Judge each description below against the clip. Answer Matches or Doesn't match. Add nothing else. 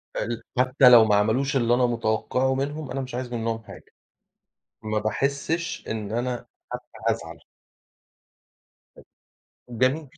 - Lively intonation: Doesn't match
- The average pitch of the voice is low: Matches